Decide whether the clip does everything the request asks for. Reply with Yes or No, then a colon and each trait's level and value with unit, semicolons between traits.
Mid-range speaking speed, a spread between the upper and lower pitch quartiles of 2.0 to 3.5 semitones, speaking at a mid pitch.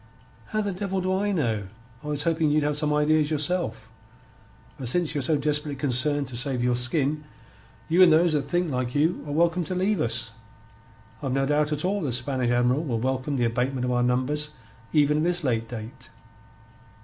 No: average, 195 wpm; average, 4.2 semitones; medium, 145 Hz